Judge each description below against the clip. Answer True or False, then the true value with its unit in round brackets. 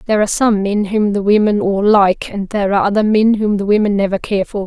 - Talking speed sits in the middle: False (255 wpm)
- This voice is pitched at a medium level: False (205 Hz)